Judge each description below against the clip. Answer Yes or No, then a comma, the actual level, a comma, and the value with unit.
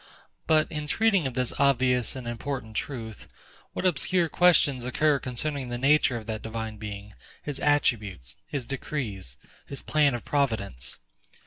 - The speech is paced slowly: No, average, 145 wpm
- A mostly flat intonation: No, average, 4.7 semitones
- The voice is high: No, low, 130 Hz